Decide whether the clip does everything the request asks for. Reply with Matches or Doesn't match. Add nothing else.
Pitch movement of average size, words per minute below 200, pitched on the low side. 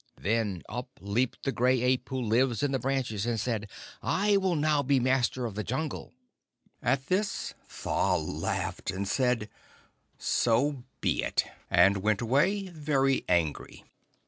Matches